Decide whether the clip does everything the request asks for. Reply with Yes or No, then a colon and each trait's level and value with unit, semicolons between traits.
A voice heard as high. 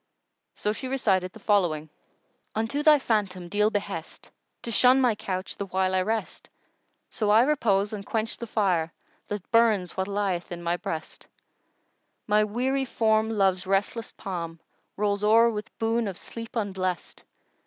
Yes: high, 205 Hz